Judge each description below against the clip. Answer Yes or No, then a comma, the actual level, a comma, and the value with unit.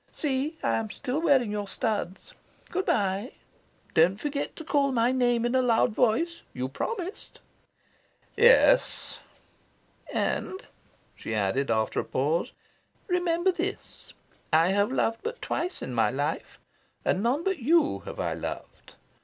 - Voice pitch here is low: No, very high, 250 Hz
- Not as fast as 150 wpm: Yes, average, 140 wpm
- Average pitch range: No, wide, 8.6 semitones